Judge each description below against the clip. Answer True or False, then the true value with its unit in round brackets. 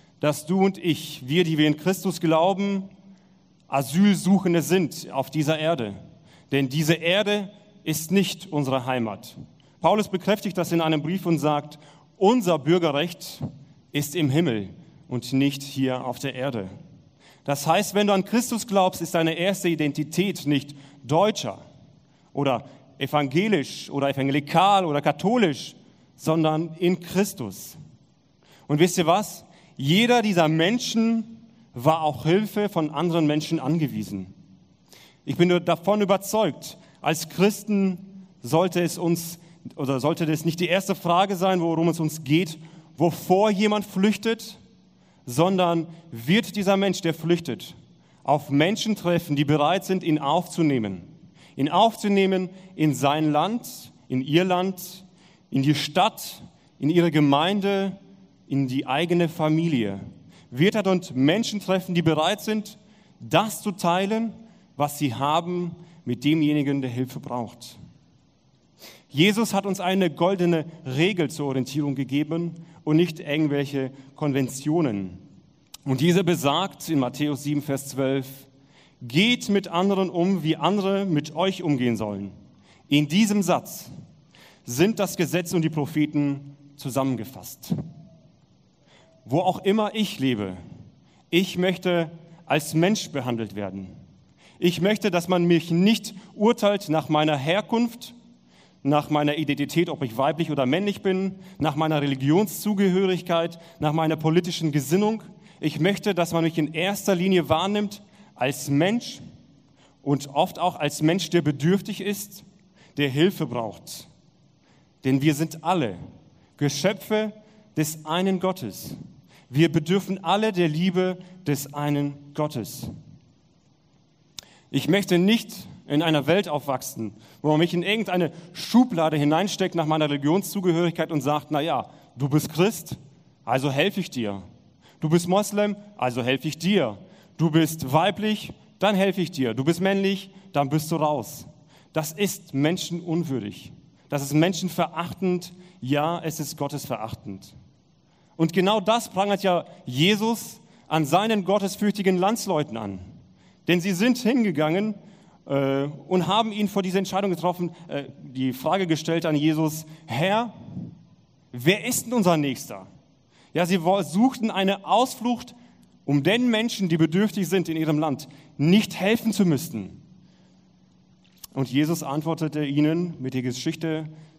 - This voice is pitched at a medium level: True (165 Hz)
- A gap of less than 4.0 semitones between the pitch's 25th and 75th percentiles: False (4.6 semitones)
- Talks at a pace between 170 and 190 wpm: False (135 wpm)